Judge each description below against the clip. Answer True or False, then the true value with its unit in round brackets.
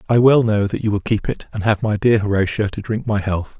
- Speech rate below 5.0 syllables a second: False (5.6 syllables/s)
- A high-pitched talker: False (105 Hz)